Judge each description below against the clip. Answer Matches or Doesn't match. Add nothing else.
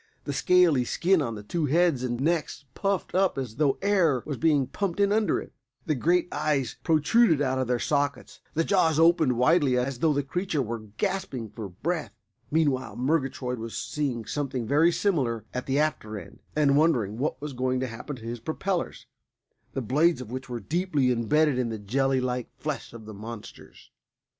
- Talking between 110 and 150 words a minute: Doesn't match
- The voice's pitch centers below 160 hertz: Matches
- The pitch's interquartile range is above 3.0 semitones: Matches